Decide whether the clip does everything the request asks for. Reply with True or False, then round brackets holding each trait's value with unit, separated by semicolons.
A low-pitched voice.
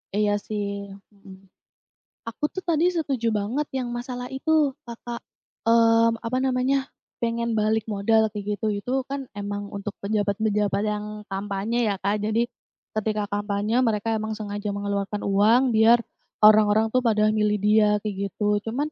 False (215 Hz)